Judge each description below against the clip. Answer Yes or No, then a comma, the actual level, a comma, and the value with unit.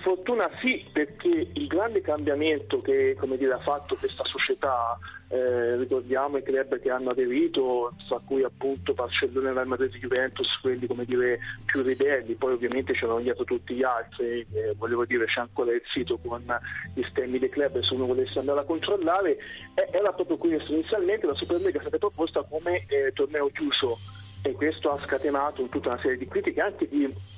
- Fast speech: Yes, fast, 180 wpm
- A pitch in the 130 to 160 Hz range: Yes, medium, 140 Hz